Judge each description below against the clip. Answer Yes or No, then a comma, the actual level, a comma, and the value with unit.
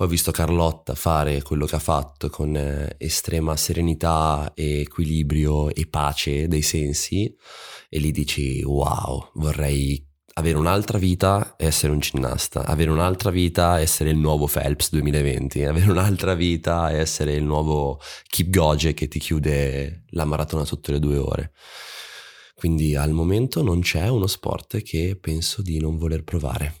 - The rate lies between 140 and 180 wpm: Yes, average, 155 wpm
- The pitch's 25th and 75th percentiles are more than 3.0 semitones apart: No, narrow, 2.5 semitones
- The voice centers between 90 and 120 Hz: No, very low, 80 Hz